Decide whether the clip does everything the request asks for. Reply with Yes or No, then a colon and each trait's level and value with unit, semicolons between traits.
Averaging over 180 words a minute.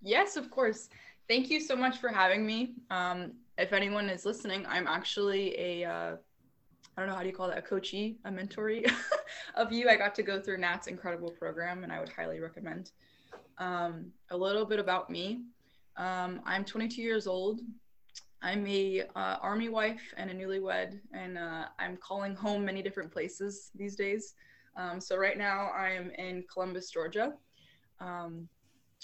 No: average, 175 wpm